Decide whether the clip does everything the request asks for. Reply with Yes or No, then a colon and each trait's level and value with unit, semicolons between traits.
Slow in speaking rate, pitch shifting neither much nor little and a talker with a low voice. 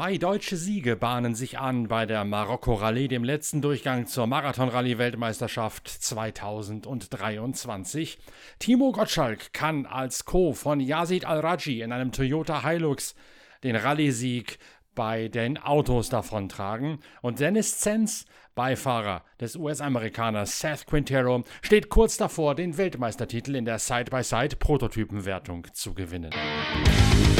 Yes: slow, 110 wpm; average, 5.0 semitones; low, 125 Hz